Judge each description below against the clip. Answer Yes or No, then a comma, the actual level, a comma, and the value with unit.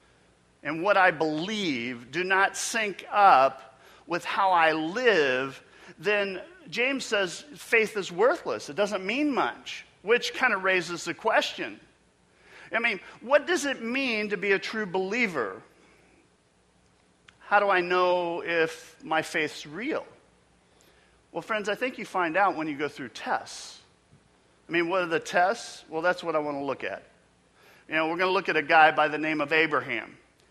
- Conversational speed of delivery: Yes, average, 170 wpm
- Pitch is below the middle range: No, medium, 170 Hz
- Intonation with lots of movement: Yes, wide, 5.7 semitones